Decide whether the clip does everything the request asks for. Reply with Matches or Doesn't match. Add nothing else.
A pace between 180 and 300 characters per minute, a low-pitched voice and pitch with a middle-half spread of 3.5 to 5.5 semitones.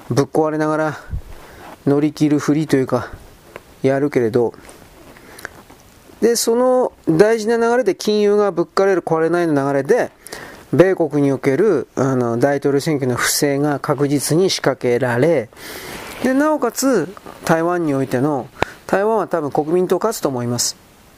Doesn't match